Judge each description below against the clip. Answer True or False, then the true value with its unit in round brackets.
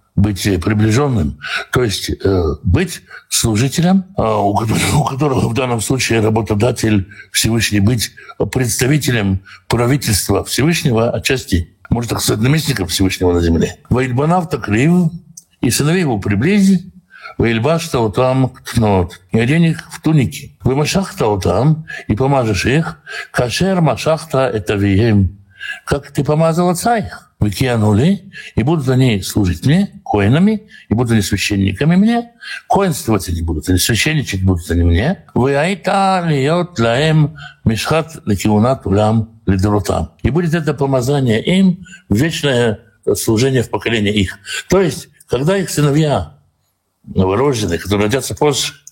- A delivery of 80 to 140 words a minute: True (120 wpm)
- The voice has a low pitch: True (125 Hz)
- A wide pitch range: True (6.8 semitones)